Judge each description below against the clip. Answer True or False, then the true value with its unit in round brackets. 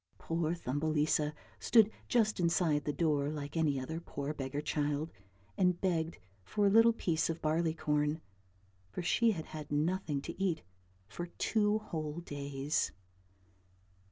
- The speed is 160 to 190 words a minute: False (140 wpm)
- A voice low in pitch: False (160 Hz)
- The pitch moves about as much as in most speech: True (3.0 semitones)